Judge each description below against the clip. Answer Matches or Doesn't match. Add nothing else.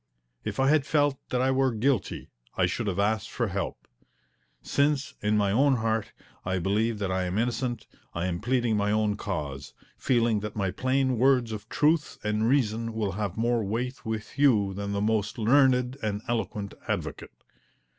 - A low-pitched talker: Matches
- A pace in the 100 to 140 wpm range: Doesn't match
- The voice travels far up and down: Doesn't match